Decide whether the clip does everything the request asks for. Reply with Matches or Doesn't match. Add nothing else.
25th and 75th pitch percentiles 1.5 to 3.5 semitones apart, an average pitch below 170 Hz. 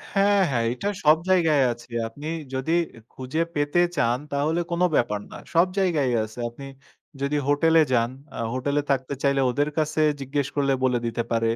Doesn't match